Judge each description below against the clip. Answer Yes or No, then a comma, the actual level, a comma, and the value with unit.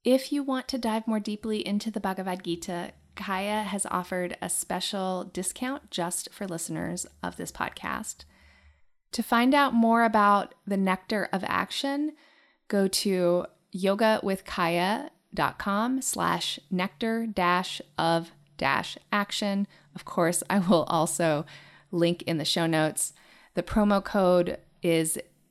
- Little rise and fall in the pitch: No, average, 4.1 semitones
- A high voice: Yes, high, 195 Hz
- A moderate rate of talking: No, slow, 130 wpm